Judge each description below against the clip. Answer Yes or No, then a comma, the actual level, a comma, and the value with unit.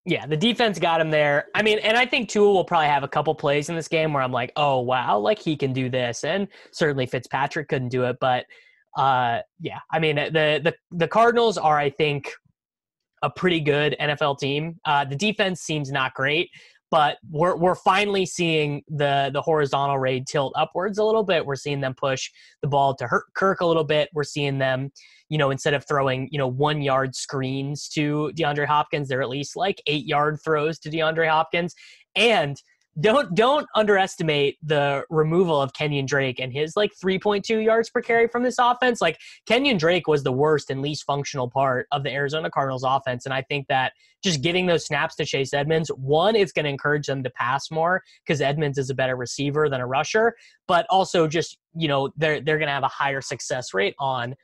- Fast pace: Yes, fast, 210 wpm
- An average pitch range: Yes, average, 3.6 semitones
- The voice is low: No, medium, 150 Hz